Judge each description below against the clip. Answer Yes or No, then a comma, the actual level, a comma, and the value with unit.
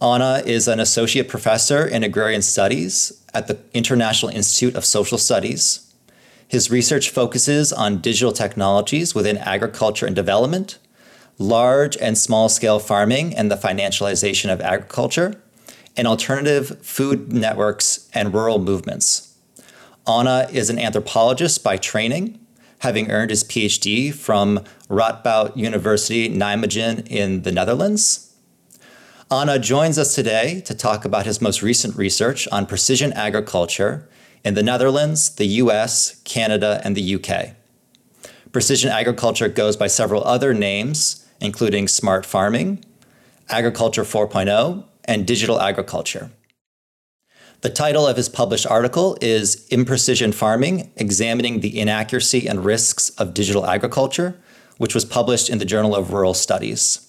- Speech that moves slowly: Yes, slow, 130 wpm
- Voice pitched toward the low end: Yes, low, 115 Hz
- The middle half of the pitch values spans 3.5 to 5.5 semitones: Yes, average, 3.9 semitones